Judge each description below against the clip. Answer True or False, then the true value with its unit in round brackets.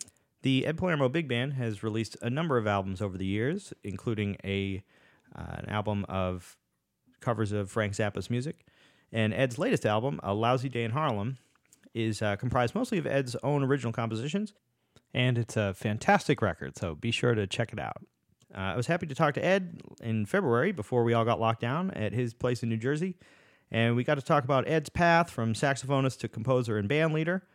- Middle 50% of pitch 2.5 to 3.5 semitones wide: False (5.0 semitones)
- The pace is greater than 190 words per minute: True (200 wpm)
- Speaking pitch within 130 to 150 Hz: False (120 Hz)